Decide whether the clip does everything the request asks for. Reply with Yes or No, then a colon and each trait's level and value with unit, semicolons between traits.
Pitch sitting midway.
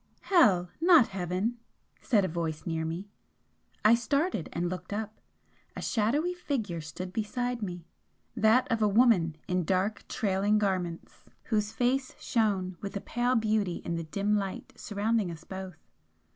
No: high, 205 Hz